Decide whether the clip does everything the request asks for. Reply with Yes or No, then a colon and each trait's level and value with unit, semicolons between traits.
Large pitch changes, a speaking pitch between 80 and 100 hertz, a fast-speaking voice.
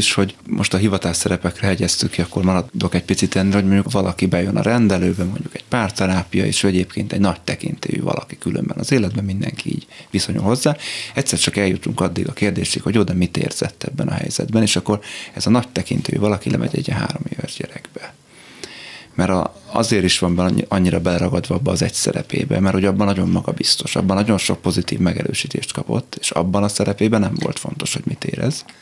No: narrow, 2.5 semitones; very low, 95 Hz; fast, 190 wpm